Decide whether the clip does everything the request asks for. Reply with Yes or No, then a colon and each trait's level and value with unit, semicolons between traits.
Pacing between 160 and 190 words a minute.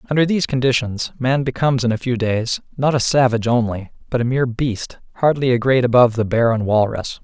No: fast, 205 wpm